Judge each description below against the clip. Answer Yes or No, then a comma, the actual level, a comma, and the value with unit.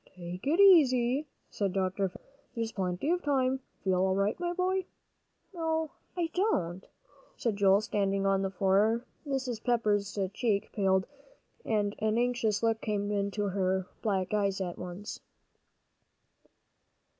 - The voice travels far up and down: No, average, 4.8 semitones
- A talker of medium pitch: No, high, 210 Hz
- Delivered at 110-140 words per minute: Yes, slow, 135 wpm